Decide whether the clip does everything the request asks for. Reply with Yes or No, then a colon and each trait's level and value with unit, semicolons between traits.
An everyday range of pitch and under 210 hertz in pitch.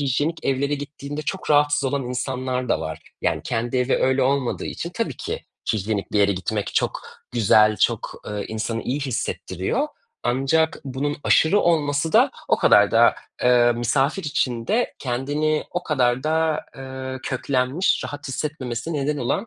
Yes: average, 3.6 semitones; low, 135 Hz